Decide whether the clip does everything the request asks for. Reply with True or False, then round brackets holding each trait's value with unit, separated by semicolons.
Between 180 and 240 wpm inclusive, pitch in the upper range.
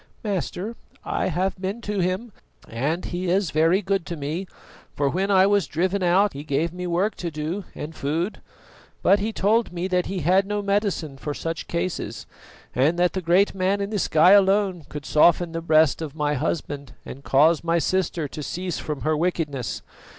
False (190 wpm; 175 Hz)